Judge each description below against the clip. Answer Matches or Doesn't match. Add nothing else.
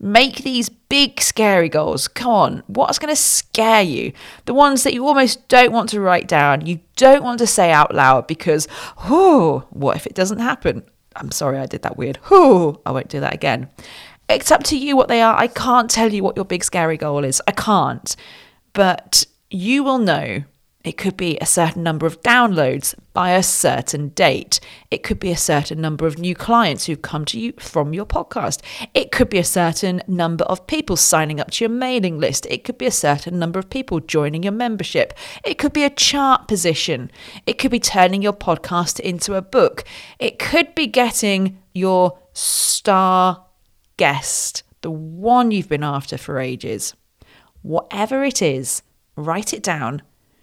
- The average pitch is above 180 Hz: Matches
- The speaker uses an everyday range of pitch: Doesn't match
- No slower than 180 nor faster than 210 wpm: Matches